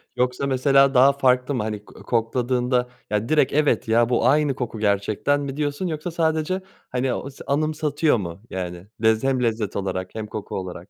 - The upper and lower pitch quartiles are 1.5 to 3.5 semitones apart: No, average, 4.7 semitones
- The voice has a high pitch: No, low, 125 Hz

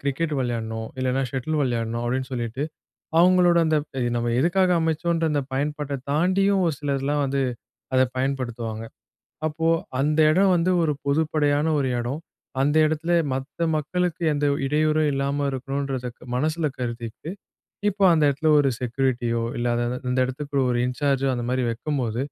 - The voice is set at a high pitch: No, medium, 140 Hz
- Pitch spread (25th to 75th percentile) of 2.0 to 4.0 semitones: Yes, average, 3.6 semitones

